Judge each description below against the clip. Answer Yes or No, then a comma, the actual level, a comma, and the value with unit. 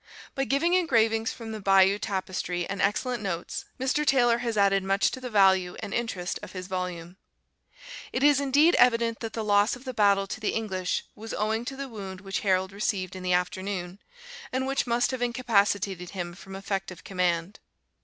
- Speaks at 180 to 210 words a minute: Yes, average, 185 wpm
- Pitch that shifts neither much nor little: Yes, average, 4.1 semitones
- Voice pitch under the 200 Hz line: No, high, 205 Hz